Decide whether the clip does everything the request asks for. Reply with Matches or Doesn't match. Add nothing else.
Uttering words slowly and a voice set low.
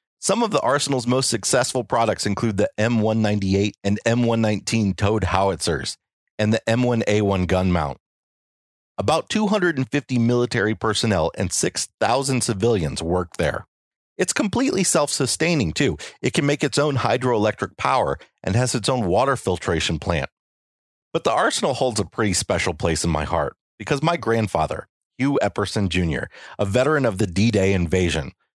Doesn't match